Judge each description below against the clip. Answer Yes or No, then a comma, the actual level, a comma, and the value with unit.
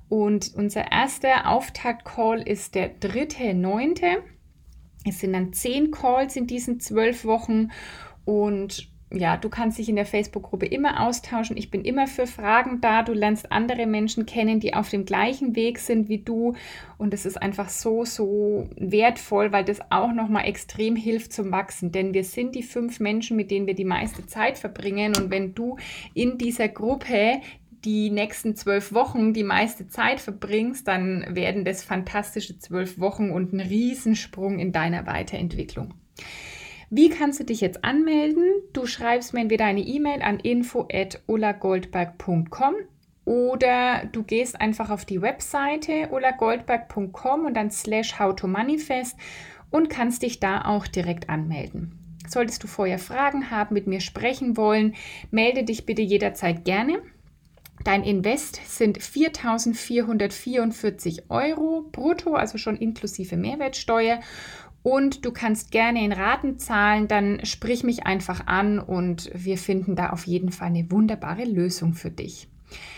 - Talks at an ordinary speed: Yes, average, 150 wpm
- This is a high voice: Yes, high, 220 Hz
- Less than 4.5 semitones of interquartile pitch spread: Yes, average, 3.5 semitones